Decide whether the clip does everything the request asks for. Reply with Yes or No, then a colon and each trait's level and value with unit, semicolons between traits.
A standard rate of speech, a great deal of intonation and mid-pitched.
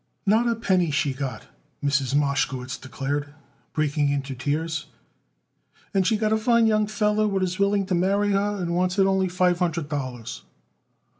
Yes: average, 170 wpm; wide, 6.0 semitones; medium, 180 Hz